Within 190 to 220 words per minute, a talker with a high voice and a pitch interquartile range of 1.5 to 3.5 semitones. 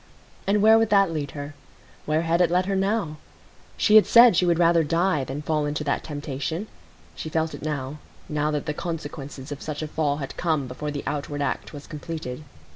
No: average, 200 wpm; medium, 155 Hz; average, 3.0 semitones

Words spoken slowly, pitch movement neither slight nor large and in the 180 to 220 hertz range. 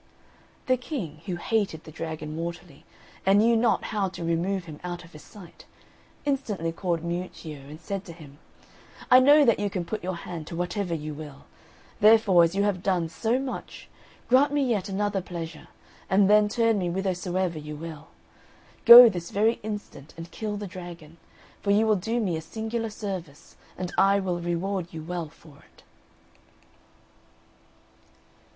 No: average, 170 wpm; average, 4.0 semitones; medium, 185 Hz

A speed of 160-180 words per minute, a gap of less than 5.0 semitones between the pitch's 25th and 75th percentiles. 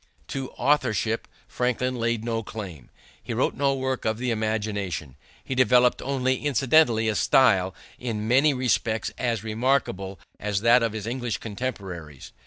No: average, 145 wpm; average, 3.1 semitones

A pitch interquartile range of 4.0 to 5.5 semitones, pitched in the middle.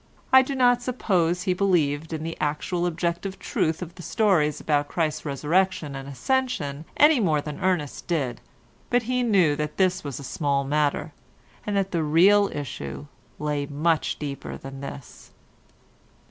Yes: average, 4.5 semitones; medium, 160 Hz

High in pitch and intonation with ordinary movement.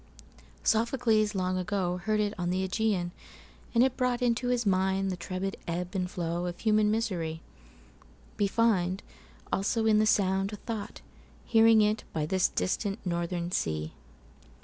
Yes: high, 195 Hz; average, 3.4 semitones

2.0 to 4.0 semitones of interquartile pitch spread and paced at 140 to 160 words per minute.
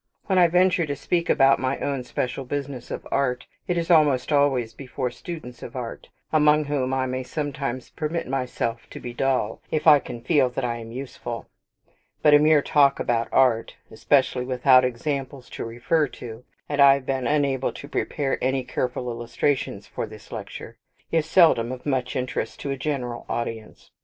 No: average, 2.8 semitones; average, 180 wpm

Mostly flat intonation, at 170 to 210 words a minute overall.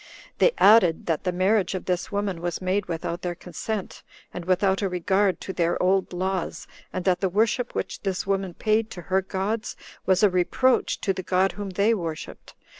Yes: narrow, 2.2 semitones; average, 190 wpm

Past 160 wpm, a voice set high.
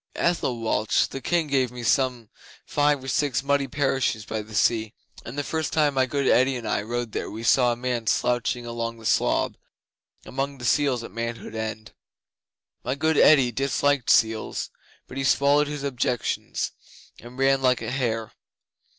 No: average, 170 wpm; low, 125 Hz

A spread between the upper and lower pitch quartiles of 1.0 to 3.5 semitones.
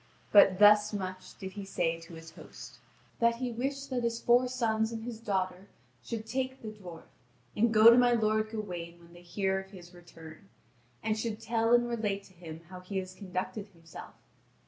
No: average, 3.9 semitones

